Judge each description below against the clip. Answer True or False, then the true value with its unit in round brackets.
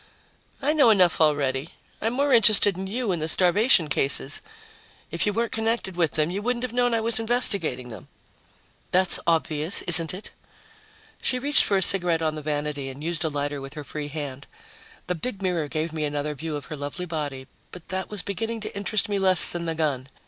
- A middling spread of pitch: False (5.7 semitones)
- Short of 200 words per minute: False (205 wpm)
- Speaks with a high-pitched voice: False (170 Hz)